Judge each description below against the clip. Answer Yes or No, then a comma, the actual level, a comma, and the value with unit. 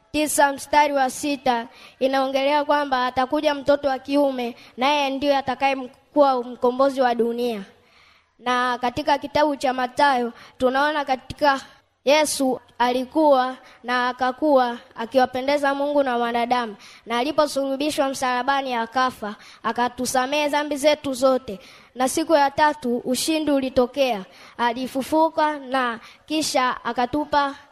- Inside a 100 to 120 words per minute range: Yes, average, 105 wpm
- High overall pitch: Yes, very high, 265 Hz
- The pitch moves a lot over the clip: No, narrow, 2.6 semitones